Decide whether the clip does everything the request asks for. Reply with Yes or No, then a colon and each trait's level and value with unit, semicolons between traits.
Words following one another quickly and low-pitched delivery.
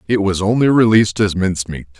Yes: fast, 210 wpm; low, 100 Hz